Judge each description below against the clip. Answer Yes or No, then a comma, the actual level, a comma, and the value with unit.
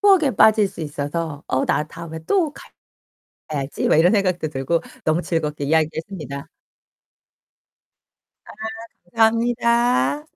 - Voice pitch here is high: No, medium, 165 Hz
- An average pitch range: No, wide, 6.7 semitones